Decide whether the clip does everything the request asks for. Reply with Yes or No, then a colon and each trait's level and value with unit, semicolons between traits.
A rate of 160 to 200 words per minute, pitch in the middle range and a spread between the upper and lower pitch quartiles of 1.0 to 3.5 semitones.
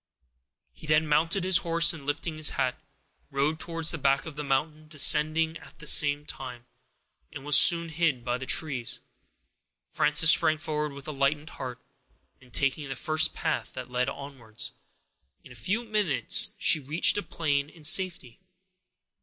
Yes: average, 165 wpm; medium, 150 Hz; average, 2.9 semitones